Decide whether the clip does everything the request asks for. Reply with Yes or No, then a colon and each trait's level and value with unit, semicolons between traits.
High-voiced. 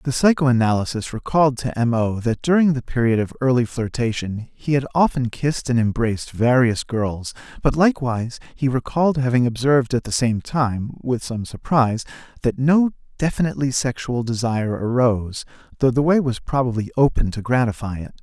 No: low, 125 Hz